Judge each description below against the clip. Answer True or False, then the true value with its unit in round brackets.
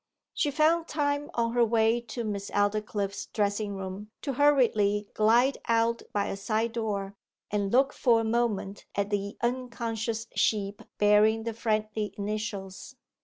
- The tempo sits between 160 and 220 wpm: False (145 wpm)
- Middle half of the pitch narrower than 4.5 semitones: True (2.6 semitones)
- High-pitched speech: True (220 Hz)